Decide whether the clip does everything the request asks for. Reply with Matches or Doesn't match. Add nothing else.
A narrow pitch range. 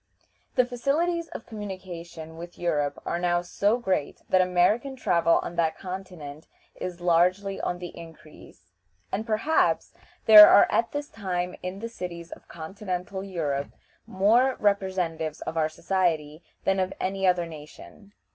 Doesn't match